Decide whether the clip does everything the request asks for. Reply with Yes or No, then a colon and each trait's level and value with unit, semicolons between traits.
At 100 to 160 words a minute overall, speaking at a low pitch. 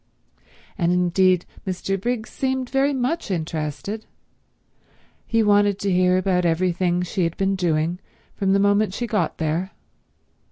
No: average, 145 wpm; high, 190 Hz